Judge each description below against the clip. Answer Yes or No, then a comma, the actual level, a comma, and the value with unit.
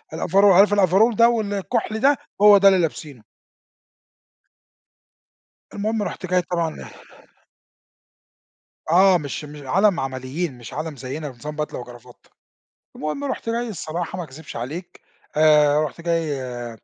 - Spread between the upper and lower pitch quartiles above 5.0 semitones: Yes, wide, 5.5 semitones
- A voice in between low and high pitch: Yes, medium, 165 Hz